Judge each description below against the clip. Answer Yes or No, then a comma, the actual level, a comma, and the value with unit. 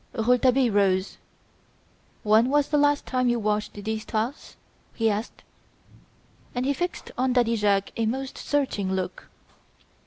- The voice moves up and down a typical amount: Yes, average, 3.9 semitones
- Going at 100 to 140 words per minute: Yes, slow, 135 wpm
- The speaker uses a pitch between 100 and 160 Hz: No, high, 230 Hz